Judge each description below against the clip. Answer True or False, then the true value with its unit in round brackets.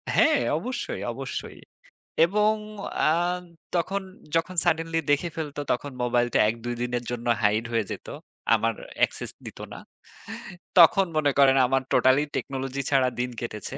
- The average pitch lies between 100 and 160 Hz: True (140 Hz)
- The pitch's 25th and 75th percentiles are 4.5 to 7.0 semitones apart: True (5.4 semitones)